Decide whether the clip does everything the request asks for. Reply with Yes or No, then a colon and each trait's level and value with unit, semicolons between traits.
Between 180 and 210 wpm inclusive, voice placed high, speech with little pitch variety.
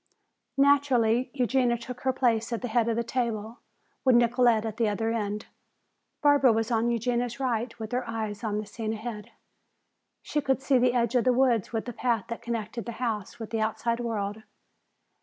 Yes: average, 190 wpm; high, 235 Hz; narrow, 2.0 semitones